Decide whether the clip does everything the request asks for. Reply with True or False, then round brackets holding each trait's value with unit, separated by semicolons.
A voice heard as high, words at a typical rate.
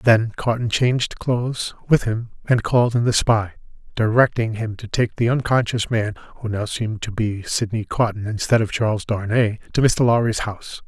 False (115 Hz; 180 wpm)